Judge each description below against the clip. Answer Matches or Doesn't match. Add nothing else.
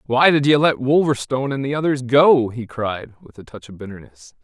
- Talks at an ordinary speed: Doesn't match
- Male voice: Matches